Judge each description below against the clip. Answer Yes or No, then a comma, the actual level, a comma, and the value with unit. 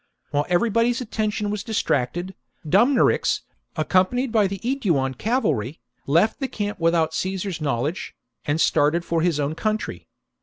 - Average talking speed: Yes, average, 150 wpm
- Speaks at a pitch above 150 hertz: Yes, medium, 185 Hz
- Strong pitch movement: Yes, wide, 5.8 semitones